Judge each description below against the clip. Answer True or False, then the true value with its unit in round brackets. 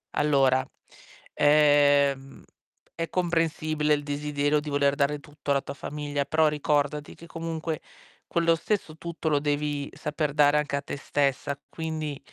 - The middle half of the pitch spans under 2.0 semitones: True (1.6 semitones)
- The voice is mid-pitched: True (150 Hz)